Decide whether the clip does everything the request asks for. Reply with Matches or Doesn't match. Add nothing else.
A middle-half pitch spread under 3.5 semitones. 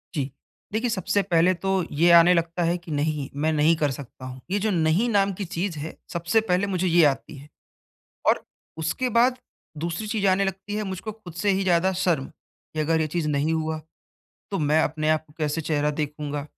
Doesn't match